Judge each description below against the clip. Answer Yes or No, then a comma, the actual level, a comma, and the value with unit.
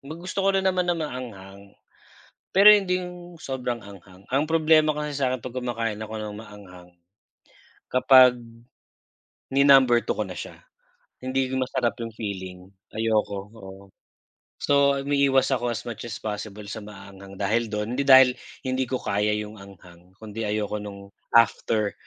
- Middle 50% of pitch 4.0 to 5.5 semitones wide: Yes, average, 4.8 semitones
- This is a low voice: Yes, low, 115 Hz